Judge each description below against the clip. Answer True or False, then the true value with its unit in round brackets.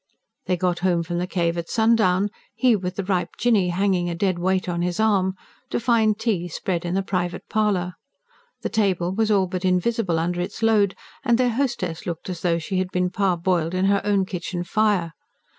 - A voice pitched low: False (185 Hz)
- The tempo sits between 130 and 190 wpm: False (200 wpm)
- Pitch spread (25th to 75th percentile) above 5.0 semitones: False (2.9 semitones)